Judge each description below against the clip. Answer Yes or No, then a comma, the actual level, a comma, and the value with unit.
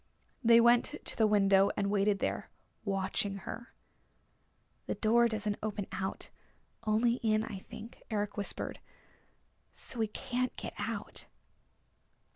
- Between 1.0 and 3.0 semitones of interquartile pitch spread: Yes, narrow, 2.6 semitones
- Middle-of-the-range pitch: No, high, 215 Hz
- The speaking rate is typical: No, slow, 125 wpm